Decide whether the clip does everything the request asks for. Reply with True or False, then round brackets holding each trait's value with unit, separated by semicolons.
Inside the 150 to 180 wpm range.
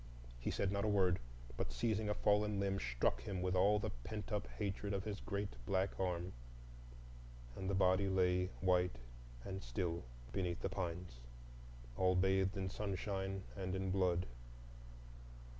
True (155 wpm)